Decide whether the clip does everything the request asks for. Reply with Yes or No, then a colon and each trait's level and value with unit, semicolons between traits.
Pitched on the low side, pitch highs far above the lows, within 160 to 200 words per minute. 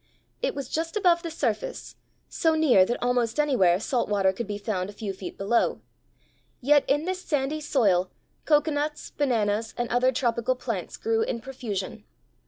No: very high, 250 Hz; wide, 6.1 semitones; average, 165 wpm